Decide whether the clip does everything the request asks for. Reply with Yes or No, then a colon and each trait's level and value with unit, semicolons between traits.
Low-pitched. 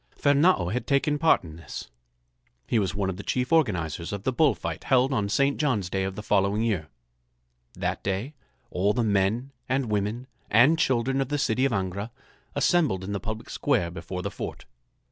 Yes: low, 110 Hz